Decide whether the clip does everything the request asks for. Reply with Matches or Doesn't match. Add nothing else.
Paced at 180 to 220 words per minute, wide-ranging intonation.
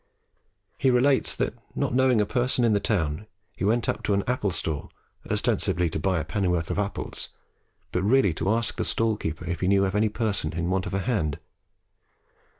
Doesn't match